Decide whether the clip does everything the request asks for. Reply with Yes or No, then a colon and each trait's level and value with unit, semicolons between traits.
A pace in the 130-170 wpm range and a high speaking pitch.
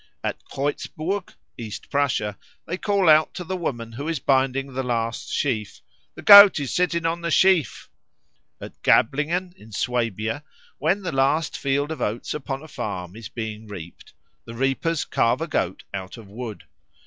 No: average, 165 wpm; low, 135 Hz